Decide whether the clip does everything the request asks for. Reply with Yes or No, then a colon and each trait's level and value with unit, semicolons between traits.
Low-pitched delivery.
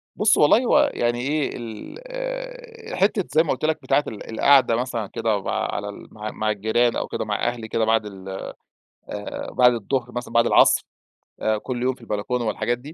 Yes: low, 120 Hz